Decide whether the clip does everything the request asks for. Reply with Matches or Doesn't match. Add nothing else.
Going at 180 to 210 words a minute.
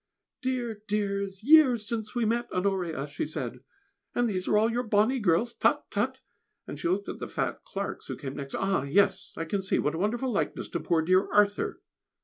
Matches